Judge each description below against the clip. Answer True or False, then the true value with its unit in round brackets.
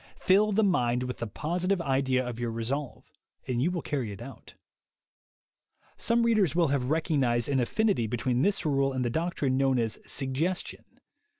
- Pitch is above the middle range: False (135 Hz)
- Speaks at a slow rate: False (175 wpm)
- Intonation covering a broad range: True (5.9 semitones)